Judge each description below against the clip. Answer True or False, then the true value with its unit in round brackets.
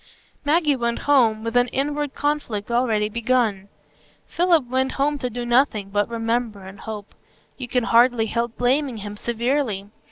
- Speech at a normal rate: True (155 wpm)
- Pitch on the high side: True (240 Hz)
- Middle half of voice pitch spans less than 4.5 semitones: True (3.5 semitones)